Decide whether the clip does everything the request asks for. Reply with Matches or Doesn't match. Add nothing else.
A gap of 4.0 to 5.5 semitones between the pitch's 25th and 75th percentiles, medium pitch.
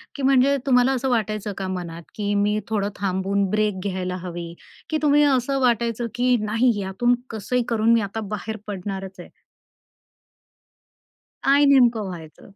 Doesn't match